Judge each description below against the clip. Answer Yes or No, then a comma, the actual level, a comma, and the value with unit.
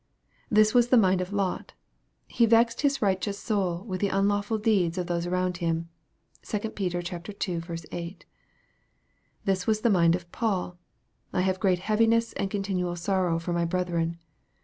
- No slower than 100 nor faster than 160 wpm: No, average, 170 wpm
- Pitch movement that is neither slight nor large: Yes, average, 3.1 semitones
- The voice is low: No, medium, 185 Hz